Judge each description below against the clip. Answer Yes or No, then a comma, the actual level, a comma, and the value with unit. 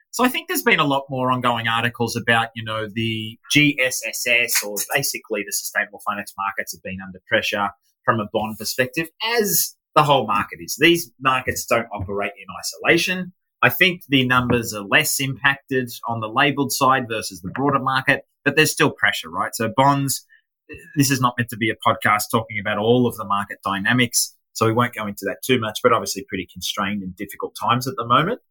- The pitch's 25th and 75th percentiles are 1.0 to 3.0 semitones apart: No, average, 4.3 semitones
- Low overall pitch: Yes, low, 120 Hz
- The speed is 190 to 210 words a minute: Yes, average, 200 wpm